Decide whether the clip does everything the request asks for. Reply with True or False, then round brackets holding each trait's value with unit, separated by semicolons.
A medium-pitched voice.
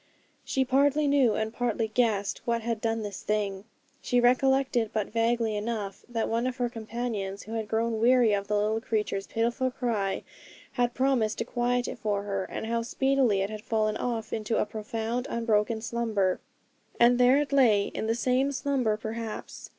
False (230 Hz)